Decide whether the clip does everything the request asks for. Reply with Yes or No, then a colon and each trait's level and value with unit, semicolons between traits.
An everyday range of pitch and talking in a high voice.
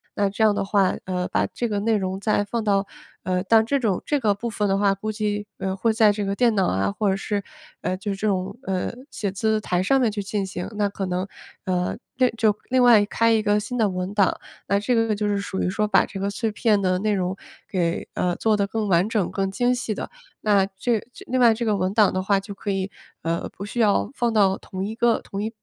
No: narrow, 2.3 semitones; high, 205 Hz